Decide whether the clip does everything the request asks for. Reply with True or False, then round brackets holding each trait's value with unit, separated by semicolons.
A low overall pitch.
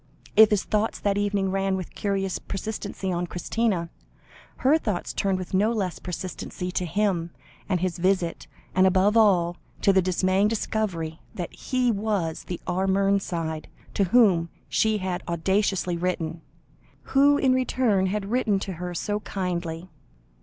False (190 Hz)